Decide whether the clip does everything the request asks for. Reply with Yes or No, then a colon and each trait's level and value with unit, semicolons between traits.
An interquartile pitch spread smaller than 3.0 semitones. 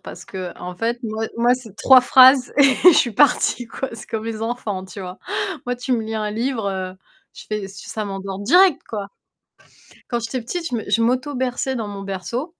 No: average, 3.9 semitones